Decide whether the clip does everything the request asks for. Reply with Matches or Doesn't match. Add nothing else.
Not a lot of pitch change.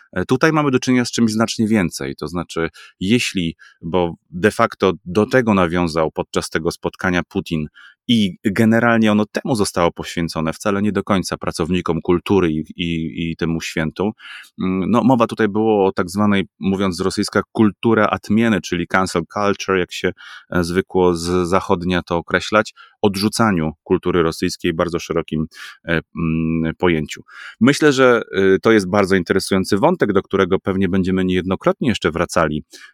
Doesn't match